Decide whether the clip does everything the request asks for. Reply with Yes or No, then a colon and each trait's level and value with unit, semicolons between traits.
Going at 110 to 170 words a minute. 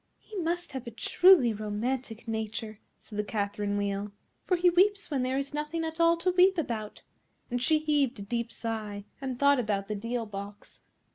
No: average, 190 wpm